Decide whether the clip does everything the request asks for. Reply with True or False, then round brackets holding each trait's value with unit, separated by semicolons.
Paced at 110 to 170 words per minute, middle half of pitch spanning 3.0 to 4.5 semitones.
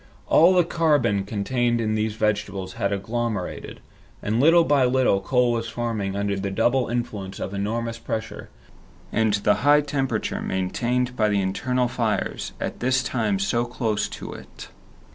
True (155 wpm; 3.7 semitones)